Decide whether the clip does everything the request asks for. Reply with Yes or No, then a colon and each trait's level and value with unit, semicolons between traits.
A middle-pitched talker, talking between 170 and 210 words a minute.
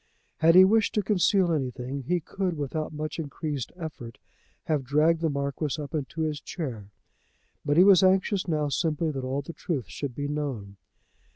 Yes: medium, 150 Hz; average, 175 wpm